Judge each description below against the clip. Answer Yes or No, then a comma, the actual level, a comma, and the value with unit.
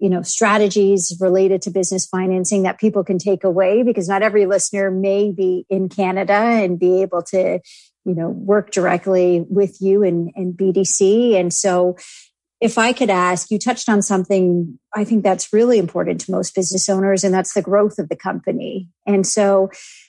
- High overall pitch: Yes, high, 195 Hz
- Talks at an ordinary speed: Yes, average, 180 wpm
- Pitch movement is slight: Yes, narrow, 1.6 semitones